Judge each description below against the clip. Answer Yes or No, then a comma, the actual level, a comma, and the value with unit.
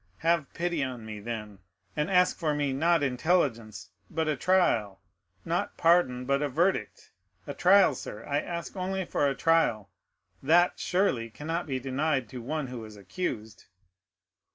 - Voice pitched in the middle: Yes, medium, 145 Hz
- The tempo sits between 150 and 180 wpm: Yes, average, 155 wpm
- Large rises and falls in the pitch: Yes, wide, 6.2 semitones